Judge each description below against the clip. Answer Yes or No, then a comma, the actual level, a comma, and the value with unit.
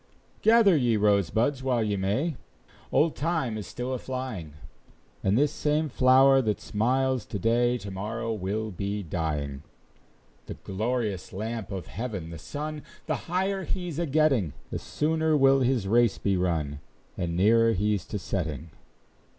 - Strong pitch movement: Yes, wide, 5.7 semitones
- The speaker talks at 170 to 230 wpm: No, average, 150 wpm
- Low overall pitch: Yes, low, 115 Hz